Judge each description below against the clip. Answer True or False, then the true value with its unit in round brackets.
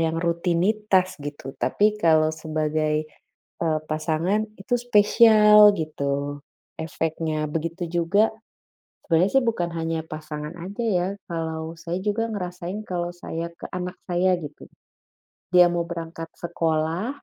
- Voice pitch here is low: False (170 Hz)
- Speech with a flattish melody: False (3.1 semitones)